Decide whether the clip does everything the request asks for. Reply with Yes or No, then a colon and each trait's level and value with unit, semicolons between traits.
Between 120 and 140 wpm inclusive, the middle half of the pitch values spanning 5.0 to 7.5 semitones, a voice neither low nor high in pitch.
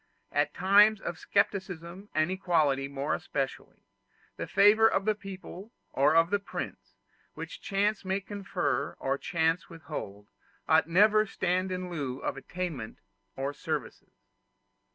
Yes: slow, 135 wpm; wide, 5.4 semitones; medium, 175 Hz